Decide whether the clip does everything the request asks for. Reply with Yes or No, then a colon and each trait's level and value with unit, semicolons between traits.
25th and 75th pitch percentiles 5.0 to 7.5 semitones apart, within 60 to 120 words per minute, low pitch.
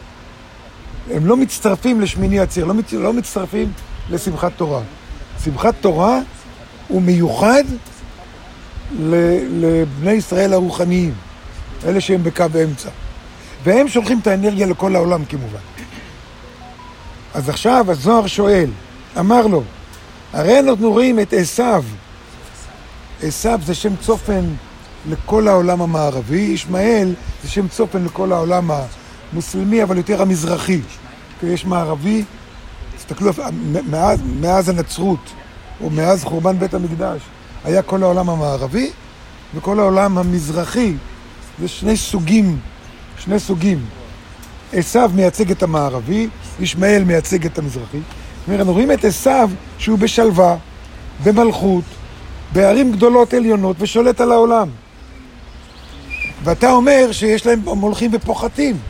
No: wide, 5.4 semitones; average, 115 wpm; medium, 185 Hz